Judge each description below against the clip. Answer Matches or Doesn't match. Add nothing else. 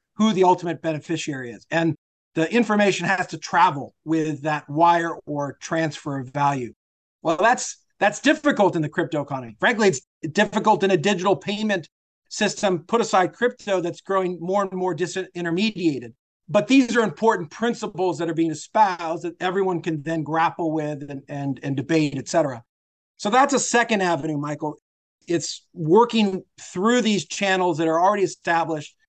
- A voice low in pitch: Doesn't match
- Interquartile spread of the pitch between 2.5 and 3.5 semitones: Doesn't match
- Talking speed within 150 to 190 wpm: Matches